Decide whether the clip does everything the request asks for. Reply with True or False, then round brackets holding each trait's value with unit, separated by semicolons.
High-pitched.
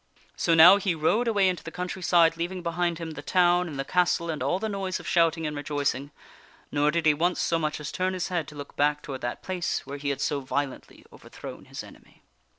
False (165 Hz)